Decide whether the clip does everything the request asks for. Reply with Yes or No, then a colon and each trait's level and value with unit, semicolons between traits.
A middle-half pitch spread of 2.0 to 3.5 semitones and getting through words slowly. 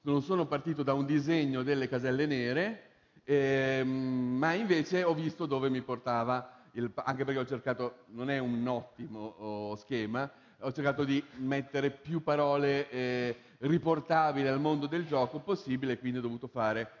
No: average, 2.9 semitones; average, 155 wpm